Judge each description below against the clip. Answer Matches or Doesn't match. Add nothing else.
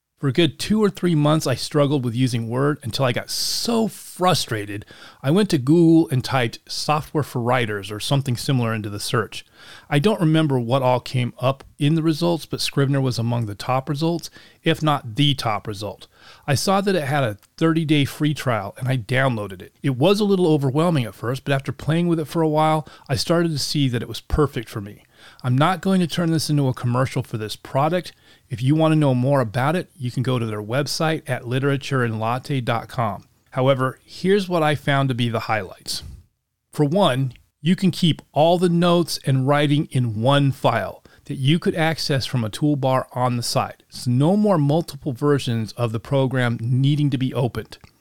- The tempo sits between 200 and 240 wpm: Matches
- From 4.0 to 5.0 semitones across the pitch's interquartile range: Matches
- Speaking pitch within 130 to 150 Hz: Matches